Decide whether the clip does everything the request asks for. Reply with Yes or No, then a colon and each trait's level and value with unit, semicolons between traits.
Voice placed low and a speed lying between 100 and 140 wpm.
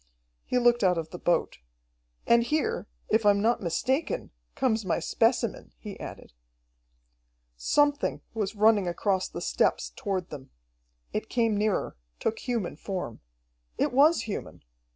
No: high, 215 Hz; slow, 135 wpm